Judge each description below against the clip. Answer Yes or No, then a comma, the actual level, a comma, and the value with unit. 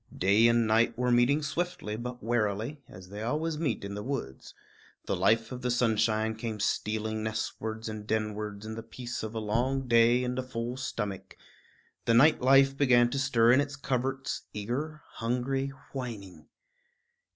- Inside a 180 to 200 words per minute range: No, average, 165 wpm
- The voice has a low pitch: Yes, low, 115 Hz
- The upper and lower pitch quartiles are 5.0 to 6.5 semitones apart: No, average, 3.3 semitones